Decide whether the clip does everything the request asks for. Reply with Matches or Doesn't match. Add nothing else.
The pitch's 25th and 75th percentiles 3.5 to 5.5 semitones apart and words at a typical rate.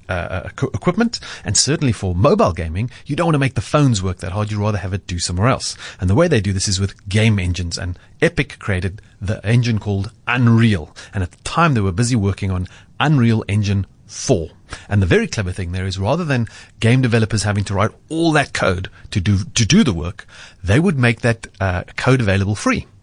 Doesn't match